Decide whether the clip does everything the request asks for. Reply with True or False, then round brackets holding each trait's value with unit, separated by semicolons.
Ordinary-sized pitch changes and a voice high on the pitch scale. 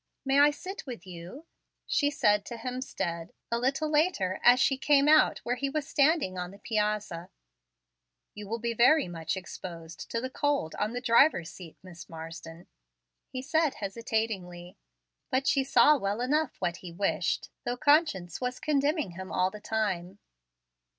False (7.3 semitones; 230 Hz)